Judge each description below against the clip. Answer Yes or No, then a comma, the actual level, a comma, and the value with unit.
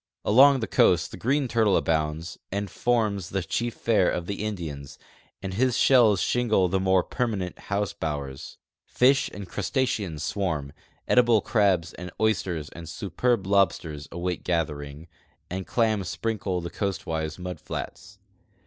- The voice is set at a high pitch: No, very low, 95 Hz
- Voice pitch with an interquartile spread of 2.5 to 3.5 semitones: No, average, 4.8 semitones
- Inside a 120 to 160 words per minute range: Yes, average, 145 wpm